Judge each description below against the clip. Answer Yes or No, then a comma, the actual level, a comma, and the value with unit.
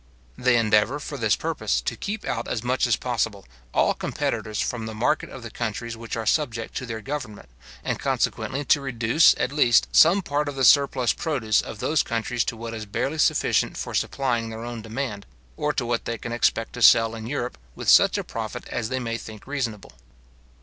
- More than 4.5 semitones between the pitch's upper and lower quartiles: No, average, 3.3 semitones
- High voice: No, low, 120 Hz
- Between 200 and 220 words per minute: Yes, fast, 205 wpm